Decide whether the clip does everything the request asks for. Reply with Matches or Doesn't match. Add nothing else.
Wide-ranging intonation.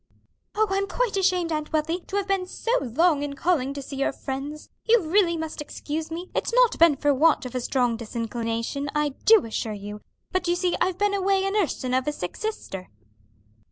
Matches